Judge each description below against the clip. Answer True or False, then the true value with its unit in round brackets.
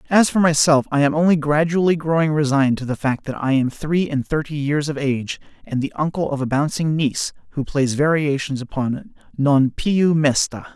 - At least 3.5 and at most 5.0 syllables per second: False (5.3 syllables/s)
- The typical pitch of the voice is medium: True (150 Hz)